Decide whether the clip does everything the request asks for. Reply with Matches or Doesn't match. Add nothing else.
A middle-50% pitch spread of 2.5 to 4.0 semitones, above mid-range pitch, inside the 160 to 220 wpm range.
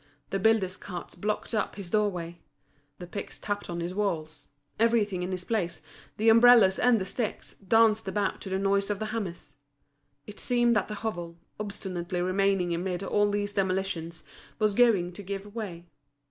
Matches